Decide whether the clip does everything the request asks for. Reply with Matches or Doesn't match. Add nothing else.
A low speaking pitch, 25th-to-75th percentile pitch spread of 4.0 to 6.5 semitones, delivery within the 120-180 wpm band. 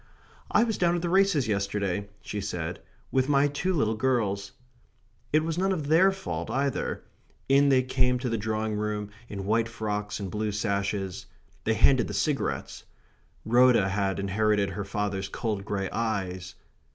Matches